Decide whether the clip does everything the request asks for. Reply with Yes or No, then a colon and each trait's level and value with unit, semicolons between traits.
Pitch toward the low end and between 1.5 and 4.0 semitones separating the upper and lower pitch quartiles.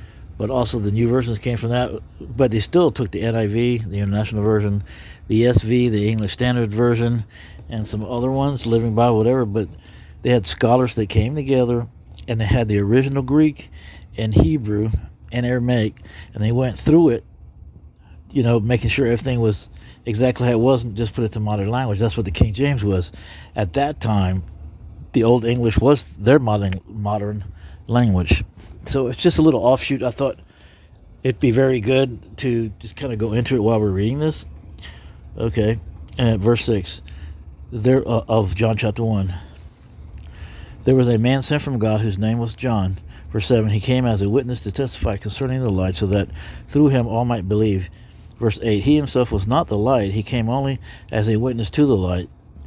Yes: low, 110 Hz; average, 3.7 semitones